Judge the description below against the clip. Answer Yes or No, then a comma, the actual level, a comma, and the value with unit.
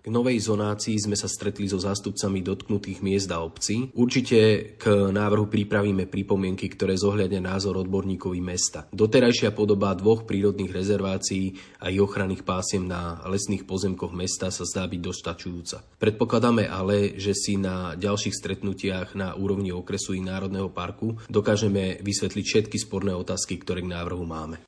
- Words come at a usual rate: Yes, average, 150 wpm